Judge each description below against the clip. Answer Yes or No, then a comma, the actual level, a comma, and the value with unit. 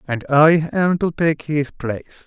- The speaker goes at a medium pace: Yes, average, 185 wpm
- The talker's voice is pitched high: No, medium, 150 Hz